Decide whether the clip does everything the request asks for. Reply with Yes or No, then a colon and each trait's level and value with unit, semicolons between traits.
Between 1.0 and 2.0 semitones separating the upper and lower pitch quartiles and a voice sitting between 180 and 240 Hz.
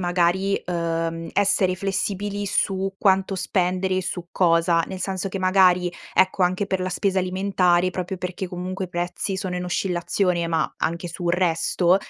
Yes: narrow, 1.4 semitones; medium, 185 Hz